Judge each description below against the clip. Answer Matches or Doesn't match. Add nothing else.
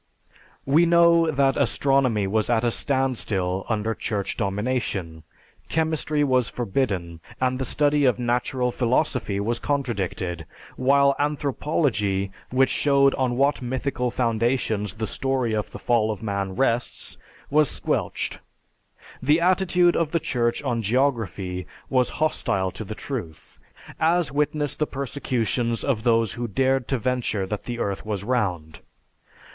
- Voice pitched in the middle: Doesn't match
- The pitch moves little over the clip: Doesn't match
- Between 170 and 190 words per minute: Doesn't match